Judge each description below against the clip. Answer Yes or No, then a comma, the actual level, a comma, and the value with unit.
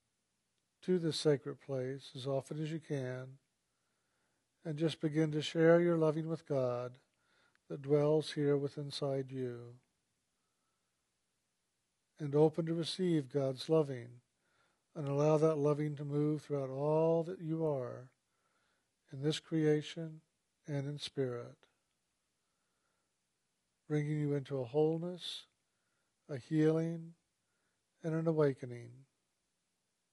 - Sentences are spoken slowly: Yes, slow, 115 wpm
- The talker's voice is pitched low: No, medium, 150 Hz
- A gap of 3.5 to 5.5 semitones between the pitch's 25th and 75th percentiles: No, average, 3.0 semitones